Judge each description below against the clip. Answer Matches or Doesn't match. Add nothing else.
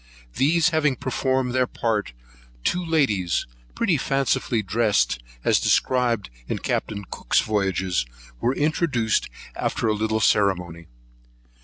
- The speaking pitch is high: Doesn't match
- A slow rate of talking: Matches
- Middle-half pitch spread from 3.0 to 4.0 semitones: Doesn't match